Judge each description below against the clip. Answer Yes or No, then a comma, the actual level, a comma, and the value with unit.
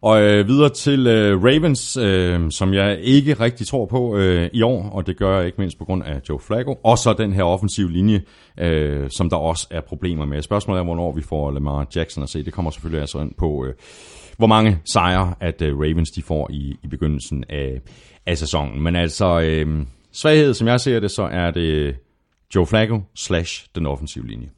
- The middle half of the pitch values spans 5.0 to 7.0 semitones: Yes, wide, 5.5 semitones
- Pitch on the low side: Yes, very low, 90 Hz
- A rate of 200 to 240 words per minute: Yes, average, 210 wpm